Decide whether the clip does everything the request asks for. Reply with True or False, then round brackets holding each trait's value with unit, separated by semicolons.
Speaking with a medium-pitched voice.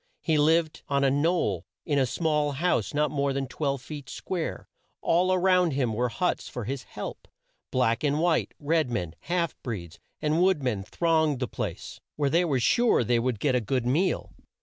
True (145 Hz)